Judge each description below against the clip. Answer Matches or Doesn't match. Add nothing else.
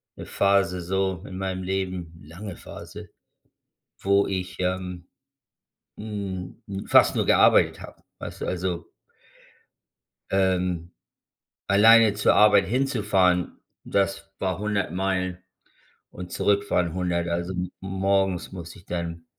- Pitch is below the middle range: Matches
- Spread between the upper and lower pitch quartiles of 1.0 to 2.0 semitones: Matches